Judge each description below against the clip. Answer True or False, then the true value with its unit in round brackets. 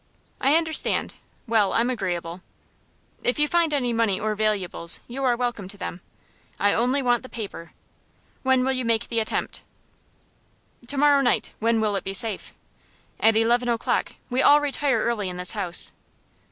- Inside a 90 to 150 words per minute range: False (165 wpm)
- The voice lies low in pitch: False (230 Hz)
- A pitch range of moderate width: True (4.1 semitones)